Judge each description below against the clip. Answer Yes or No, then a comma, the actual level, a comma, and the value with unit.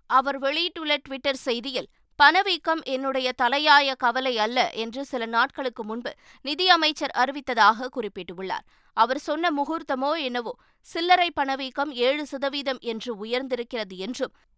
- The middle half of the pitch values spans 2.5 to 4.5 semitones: Yes, average, 2.8 semitones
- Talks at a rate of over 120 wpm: No, average, 110 wpm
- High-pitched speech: Yes, very high, 270 Hz